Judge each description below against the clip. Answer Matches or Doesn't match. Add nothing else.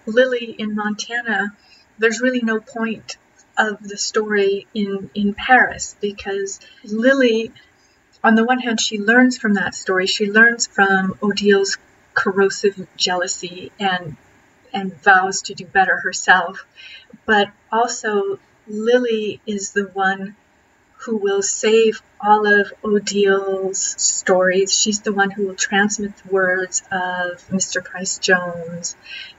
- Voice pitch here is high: Matches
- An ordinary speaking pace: Doesn't match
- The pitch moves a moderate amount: Doesn't match